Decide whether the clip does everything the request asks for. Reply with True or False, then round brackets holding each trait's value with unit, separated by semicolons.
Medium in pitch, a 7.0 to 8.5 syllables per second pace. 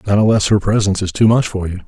False (100 Hz; 7.1 syllables/s)